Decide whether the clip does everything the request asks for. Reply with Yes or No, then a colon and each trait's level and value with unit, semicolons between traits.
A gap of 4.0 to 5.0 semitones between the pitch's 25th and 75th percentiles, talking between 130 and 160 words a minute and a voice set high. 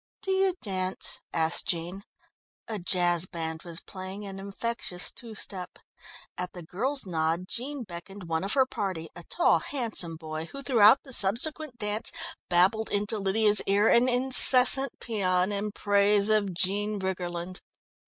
Yes: average, 4.3 semitones; average, 150 wpm; high, 200 Hz